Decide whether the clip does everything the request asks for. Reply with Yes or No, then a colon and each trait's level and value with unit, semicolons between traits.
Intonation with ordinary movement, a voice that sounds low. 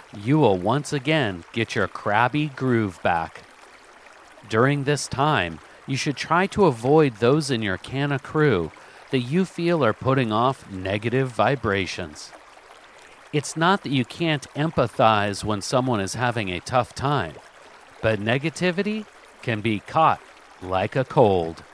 No: wide, 5.7 semitones; low, 130 Hz